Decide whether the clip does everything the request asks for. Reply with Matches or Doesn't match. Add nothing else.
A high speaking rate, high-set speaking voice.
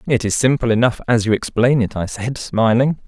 Doesn't match